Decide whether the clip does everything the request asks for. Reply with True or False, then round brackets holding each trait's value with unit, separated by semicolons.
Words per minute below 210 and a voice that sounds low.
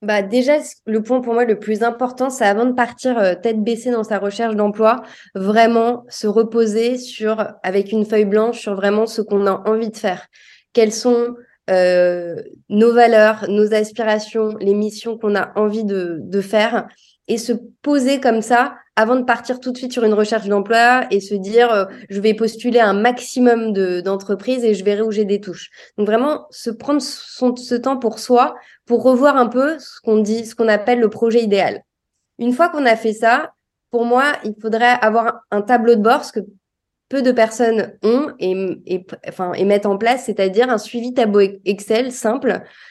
False (195 wpm; 225 Hz)